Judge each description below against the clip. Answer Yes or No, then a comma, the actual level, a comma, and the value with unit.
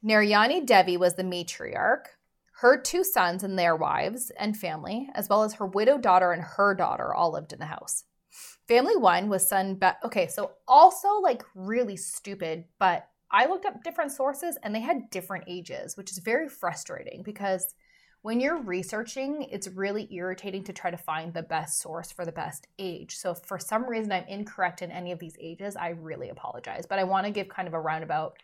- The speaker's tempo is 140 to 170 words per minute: No, average, 200 wpm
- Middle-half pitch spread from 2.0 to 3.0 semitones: No, average, 3.7 semitones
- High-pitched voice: Yes, high, 195 Hz